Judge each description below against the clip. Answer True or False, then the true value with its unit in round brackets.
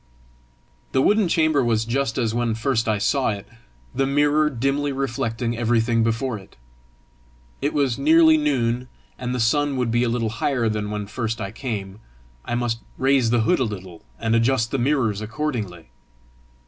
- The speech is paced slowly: False (170 wpm)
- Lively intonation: False (3.5 semitones)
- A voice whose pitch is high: False (120 Hz)